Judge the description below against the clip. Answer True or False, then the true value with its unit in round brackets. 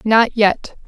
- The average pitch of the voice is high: True (220 Hz)